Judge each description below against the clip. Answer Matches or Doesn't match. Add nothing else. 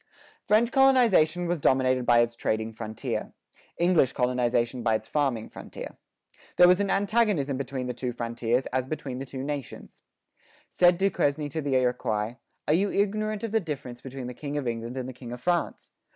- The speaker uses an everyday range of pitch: Doesn't match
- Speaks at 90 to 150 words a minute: Doesn't match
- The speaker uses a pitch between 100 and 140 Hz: Matches